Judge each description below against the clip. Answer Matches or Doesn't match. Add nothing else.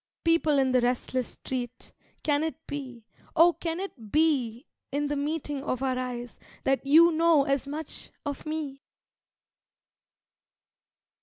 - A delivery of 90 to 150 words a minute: Matches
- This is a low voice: Doesn't match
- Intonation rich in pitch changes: Doesn't match